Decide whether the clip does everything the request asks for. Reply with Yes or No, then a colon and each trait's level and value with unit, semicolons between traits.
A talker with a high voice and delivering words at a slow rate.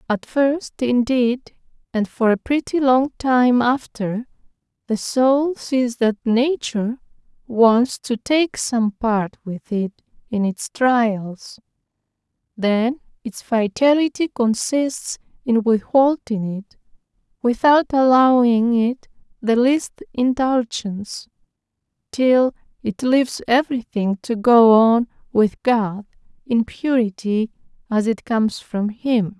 Yes: high, 240 Hz; slow, 110 wpm